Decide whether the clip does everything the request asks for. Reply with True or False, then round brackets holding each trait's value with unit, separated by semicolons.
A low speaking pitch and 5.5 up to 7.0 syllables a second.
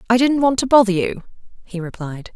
False (215 Hz; 5.6 syllables/s)